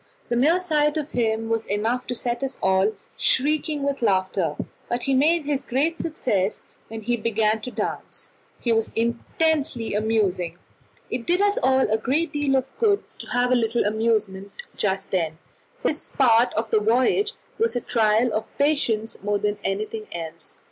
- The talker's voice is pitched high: Yes, high, 235 Hz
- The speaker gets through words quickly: No, average, 170 wpm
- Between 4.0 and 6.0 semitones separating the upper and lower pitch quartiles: Yes, average, 4.6 semitones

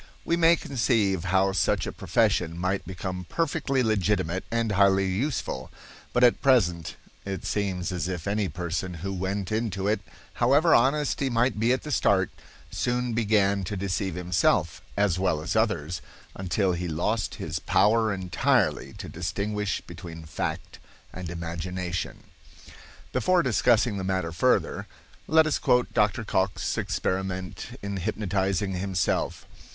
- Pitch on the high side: No, very low, 95 Hz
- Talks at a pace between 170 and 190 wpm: No, average, 140 wpm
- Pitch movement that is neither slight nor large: Yes, average, 3.8 semitones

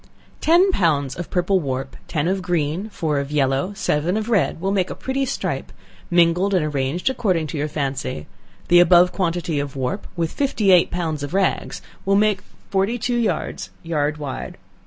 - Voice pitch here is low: No, medium, 175 Hz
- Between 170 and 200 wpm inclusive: Yes, average, 180 wpm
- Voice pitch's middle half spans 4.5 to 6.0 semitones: Yes, average, 4.9 semitones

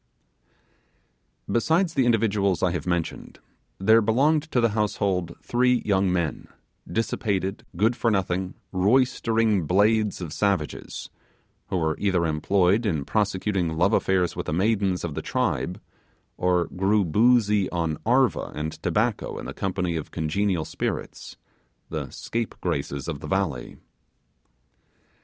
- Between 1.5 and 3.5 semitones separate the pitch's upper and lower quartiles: No, average, 4.1 semitones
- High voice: No, very low, 95 Hz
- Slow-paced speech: Yes, slow, 130 wpm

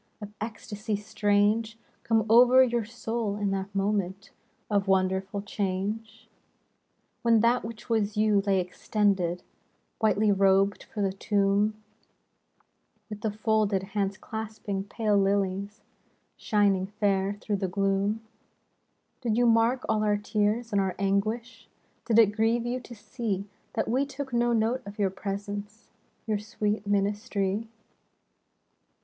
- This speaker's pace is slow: Yes, slow, 130 wpm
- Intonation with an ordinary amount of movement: No, narrow, 2.1 semitones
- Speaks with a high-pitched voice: Yes, high, 210 Hz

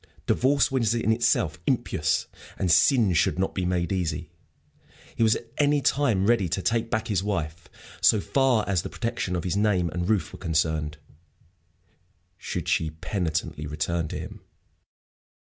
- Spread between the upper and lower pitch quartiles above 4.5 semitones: Yes, average, 5.3 semitones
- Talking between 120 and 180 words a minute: Yes, average, 160 wpm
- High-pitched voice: No, very low, 95 Hz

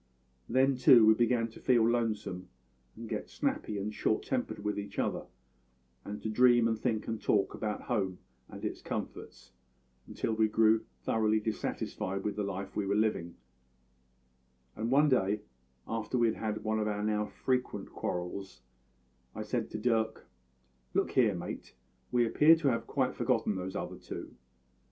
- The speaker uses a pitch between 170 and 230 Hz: No, low, 110 Hz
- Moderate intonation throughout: No, narrow, 2.3 semitones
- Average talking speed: Yes, average, 165 wpm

